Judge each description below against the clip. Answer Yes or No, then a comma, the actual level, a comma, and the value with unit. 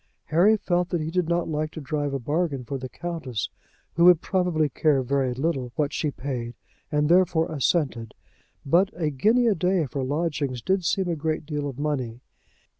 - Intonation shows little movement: No, average, 4.0 semitones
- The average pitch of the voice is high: No, medium, 155 Hz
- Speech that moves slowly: No, average, 190 wpm